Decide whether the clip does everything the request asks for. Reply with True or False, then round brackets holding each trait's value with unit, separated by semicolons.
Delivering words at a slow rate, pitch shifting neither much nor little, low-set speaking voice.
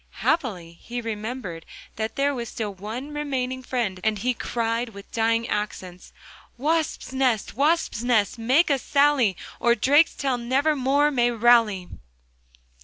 False (130 wpm; 3.9 semitones; 240 Hz)